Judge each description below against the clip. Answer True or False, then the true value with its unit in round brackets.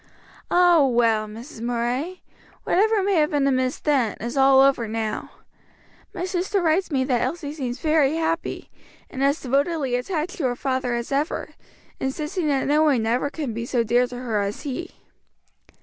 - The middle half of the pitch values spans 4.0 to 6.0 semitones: True (4.6 semitones)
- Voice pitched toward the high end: True (275 Hz)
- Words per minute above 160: True (170 wpm)